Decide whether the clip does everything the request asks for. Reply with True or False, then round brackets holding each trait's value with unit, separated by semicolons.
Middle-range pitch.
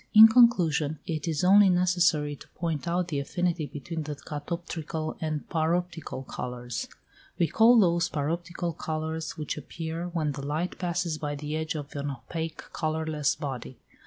True (160 Hz)